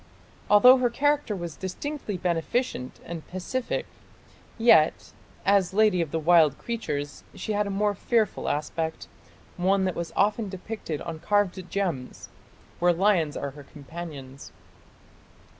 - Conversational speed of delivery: No, slow, 130 wpm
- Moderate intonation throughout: Yes, average, 4.5 semitones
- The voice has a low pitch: No, medium, 185 Hz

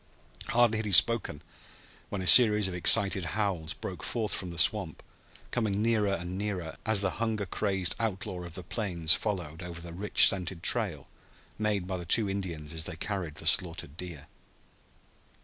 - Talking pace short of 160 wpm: No, average, 170 wpm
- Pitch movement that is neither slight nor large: Yes, average, 3.6 semitones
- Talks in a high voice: No, very low, 95 Hz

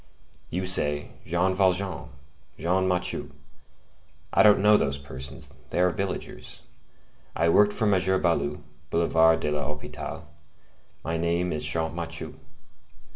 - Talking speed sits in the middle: No, slow, 120 wpm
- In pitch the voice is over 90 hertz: No, very low, 85 Hz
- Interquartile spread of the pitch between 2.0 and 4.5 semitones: Yes, average, 3.8 semitones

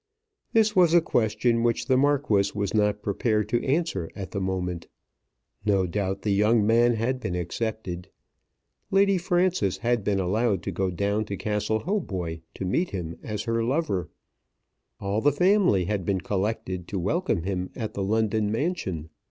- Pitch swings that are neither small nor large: Yes, average, 4.2 semitones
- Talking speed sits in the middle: Yes, average, 165 wpm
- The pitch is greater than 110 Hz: No, low, 105 Hz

